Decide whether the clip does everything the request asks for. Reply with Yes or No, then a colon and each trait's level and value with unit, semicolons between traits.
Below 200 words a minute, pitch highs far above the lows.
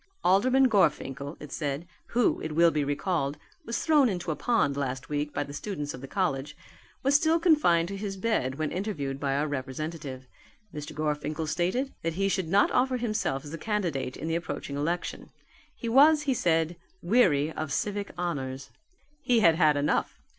Yes: average, 180 wpm; wide, 6.3 semitones